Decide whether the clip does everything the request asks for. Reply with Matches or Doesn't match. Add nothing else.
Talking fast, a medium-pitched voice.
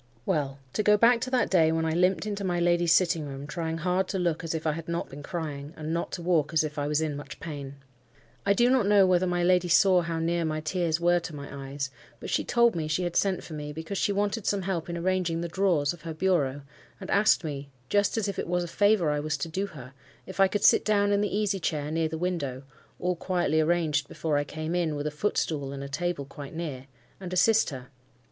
Matches